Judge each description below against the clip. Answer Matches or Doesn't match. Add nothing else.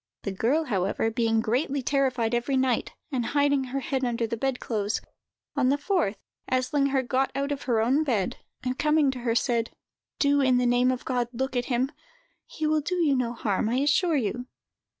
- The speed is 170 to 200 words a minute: Matches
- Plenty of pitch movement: Doesn't match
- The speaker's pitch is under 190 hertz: Doesn't match